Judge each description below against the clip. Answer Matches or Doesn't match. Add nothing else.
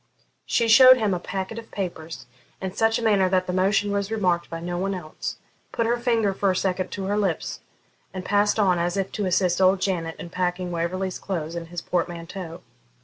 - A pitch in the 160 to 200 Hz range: Matches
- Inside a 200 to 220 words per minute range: Matches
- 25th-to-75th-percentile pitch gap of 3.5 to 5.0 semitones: Doesn't match